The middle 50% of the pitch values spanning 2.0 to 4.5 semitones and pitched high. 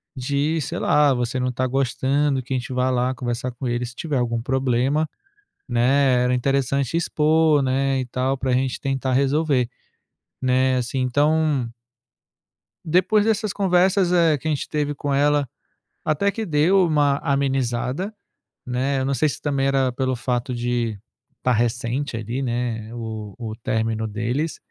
No: average, 3.1 semitones; low, 130 Hz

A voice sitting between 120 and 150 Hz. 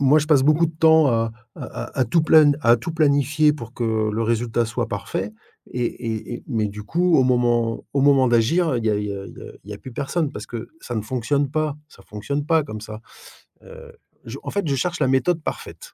Yes: low, 130 Hz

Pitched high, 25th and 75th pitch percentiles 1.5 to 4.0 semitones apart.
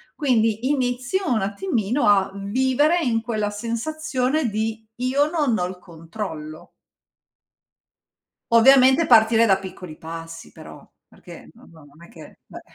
No: high, 225 Hz; average, 5.2 semitones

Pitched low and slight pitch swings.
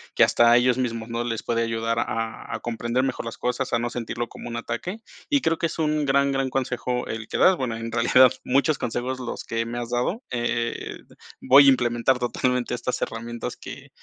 Yes: low, 120 Hz; narrow, 2.0 semitones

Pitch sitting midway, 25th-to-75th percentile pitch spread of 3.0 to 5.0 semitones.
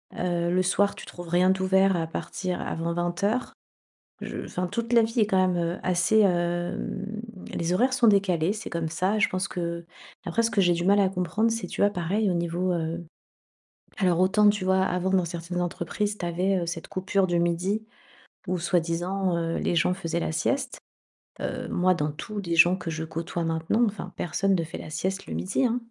No: medium, 180 Hz; narrow, 2.4 semitones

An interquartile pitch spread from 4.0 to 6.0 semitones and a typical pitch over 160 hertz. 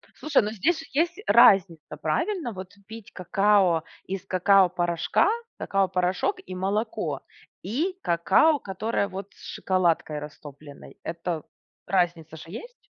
Yes: average, 4.7 semitones; high, 190 Hz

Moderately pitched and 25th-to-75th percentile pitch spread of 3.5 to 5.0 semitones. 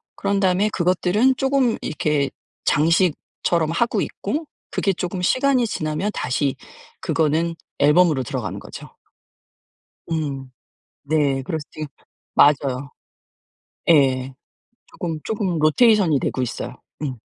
No: medium, 165 Hz; wide, 5.4 semitones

